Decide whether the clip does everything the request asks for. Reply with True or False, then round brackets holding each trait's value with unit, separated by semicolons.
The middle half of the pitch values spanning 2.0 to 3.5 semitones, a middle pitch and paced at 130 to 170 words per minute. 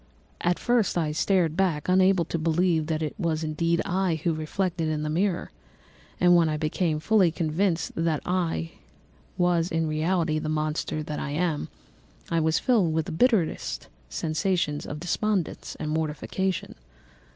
True (2.7 semitones; 165 Hz; 160 wpm)